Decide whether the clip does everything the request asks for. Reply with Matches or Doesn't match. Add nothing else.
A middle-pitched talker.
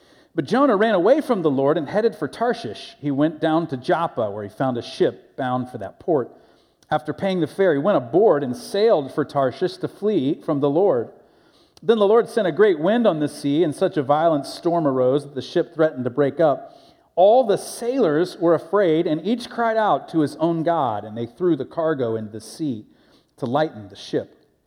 Matches